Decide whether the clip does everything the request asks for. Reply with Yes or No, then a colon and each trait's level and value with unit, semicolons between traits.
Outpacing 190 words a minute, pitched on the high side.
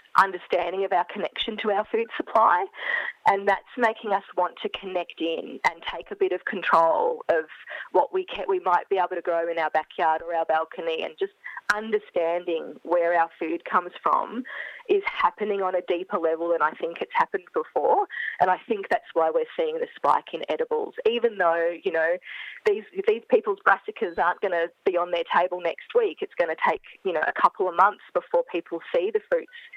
Yes: fast, 205 wpm; high, 205 Hz